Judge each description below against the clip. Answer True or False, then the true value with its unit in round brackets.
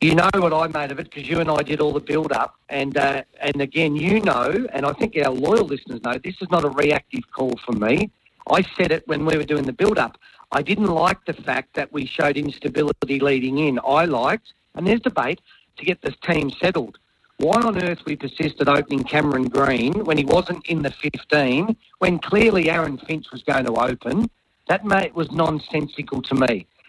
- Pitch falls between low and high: True (150 Hz)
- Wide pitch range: False (3.2 semitones)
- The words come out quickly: True (215 wpm)